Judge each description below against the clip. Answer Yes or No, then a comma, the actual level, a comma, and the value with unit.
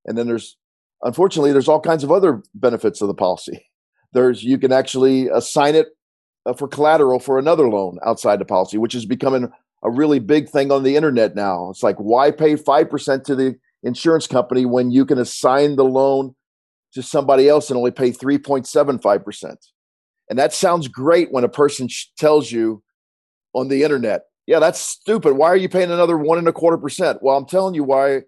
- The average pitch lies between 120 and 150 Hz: Yes, low, 135 Hz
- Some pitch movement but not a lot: Yes, average, 3.4 semitones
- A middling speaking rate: Yes, average, 190 wpm